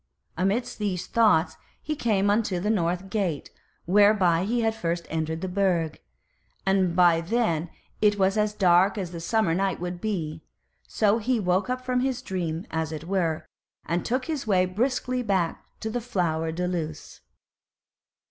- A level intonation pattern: No, average, 4.3 semitones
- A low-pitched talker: No, high, 190 Hz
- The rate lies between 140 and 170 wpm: Yes, average, 165 wpm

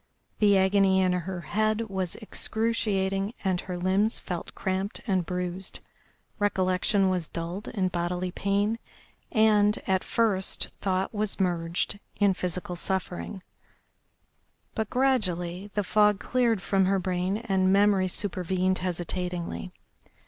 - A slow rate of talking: Yes, slow, 120 wpm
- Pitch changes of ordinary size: No, narrow, 2.2 semitones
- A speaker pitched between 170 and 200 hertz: Yes, high, 190 Hz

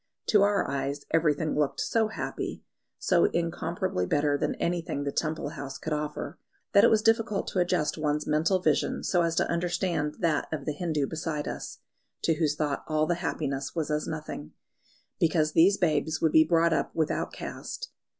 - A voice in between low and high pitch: Yes, medium, 160 Hz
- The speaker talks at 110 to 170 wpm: No, average, 180 wpm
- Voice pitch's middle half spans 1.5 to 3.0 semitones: Yes, average, 2.7 semitones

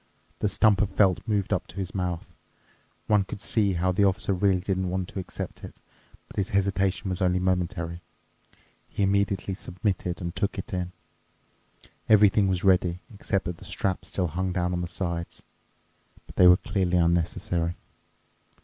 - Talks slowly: No, average, 165 wpm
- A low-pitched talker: Yes, very low, 95 Hz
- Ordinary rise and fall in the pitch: No, narrow, 1.8 semitones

